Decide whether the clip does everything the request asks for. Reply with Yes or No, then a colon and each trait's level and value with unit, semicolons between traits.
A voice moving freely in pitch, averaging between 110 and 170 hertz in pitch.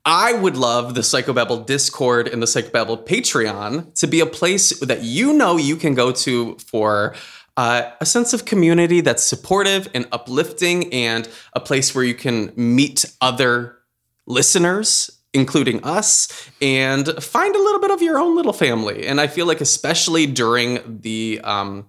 Yes: wide, 6.1 semitones; low, 135 Hz